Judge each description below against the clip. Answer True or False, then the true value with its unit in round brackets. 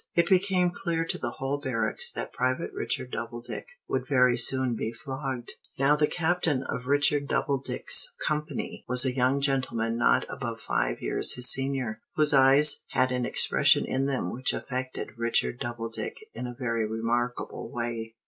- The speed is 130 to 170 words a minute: True (165 wpm)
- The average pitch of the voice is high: False (130 Hz)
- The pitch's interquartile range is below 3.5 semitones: True (3.0 semitones)